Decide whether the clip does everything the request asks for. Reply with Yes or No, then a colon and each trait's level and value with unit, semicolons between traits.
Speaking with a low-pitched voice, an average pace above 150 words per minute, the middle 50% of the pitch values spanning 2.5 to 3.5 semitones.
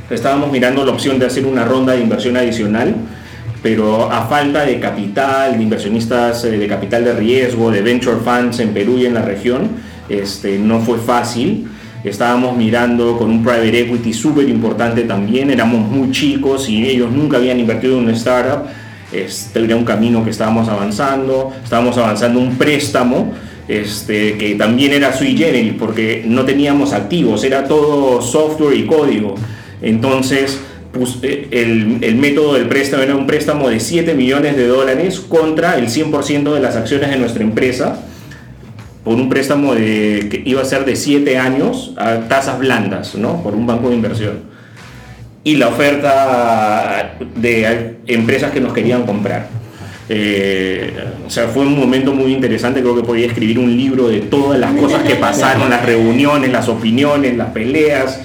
Yes: low, 120 Hz; average, 165 wpm; average, 3.1 semitones